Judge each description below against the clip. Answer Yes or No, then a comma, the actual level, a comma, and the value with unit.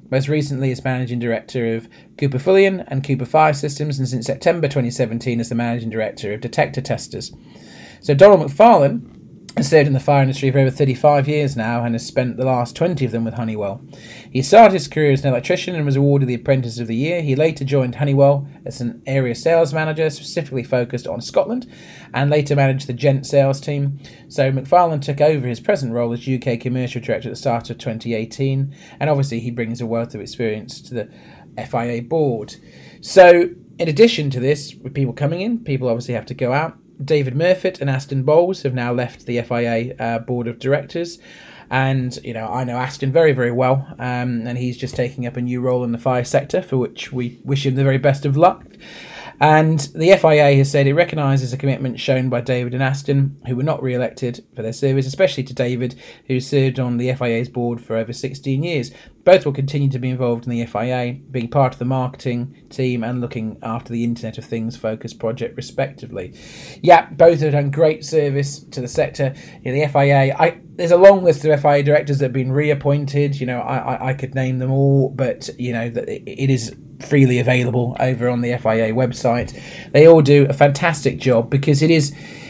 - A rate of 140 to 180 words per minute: No, fast, 205 wpm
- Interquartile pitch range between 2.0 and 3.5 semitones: Yes, average, 3.0 semitones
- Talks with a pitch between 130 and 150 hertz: Yes, low, 135 Hz